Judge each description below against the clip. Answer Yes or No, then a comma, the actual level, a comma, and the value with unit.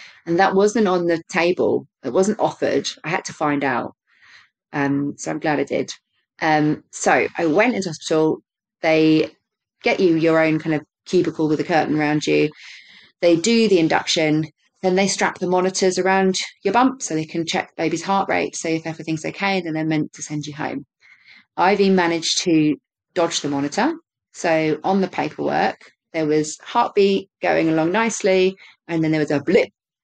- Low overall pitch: No, medium, 165 Hz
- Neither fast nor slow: Yes, average, 185 wpm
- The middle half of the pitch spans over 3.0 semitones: Yes, average, 3.5 semitones